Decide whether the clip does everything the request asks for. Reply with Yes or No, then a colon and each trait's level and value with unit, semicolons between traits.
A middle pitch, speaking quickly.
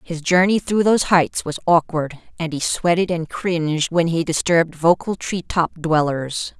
No: medium, 165 Hz; average, 165 wpm